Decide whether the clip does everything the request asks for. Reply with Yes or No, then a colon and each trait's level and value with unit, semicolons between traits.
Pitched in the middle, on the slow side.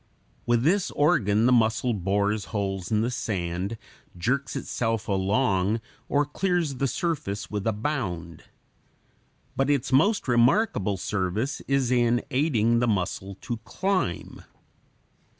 No: low, 115 Hz; slow, 125 wpm